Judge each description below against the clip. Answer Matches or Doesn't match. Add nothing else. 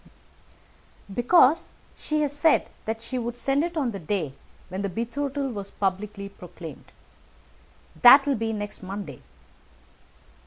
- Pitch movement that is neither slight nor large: Doesn't match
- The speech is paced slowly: Matches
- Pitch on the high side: Matches